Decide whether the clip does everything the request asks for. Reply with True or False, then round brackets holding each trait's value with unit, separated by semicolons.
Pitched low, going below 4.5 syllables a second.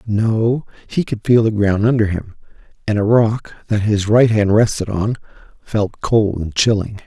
True (105 Hz; 4.3 syllables/s)